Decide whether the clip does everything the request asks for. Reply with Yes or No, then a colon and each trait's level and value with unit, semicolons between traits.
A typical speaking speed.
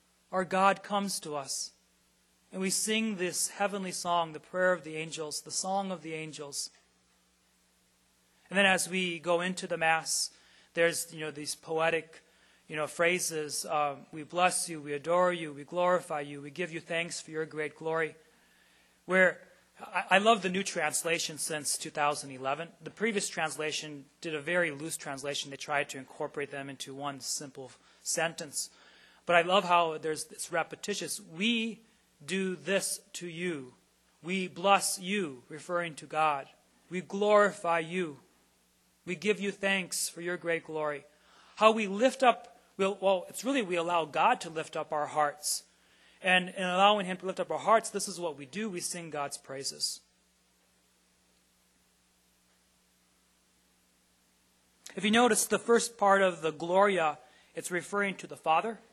Yes: average, 160 wpm